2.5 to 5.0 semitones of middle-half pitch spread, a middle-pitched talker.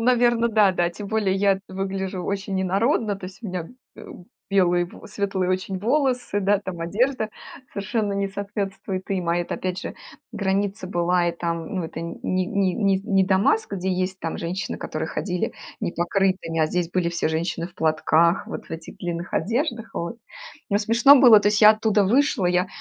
No: average, 2.8 semitones; high, 195 Hz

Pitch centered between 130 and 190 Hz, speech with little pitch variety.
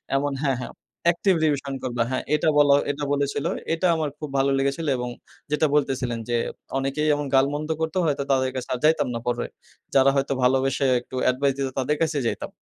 Yes: medium, 140 Hz; narrow, 2.2 semitones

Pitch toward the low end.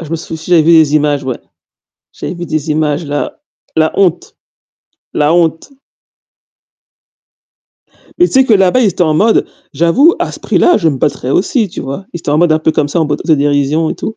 No: medium, 160 Hz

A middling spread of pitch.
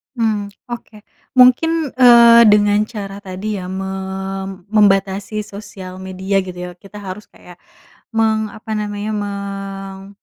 No: narrow, 2.0 semitones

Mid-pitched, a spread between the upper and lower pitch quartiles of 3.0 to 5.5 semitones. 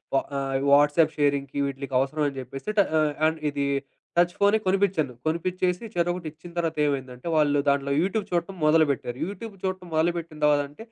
Yes: medium, 155 Hz; average, 3.8 semitones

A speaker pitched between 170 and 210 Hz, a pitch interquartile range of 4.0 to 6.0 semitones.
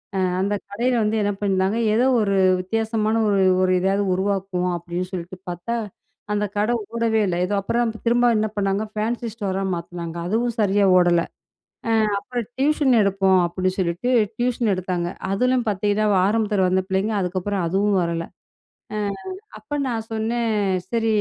No: high, 205 Hz; average, 3.3 semitones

